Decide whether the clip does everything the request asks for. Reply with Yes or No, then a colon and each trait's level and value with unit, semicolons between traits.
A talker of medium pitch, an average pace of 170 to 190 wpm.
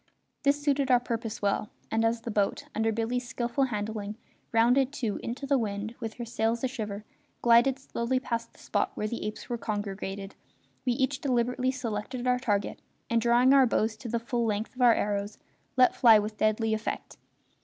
No: high, 230 Hz; average, 185 wpm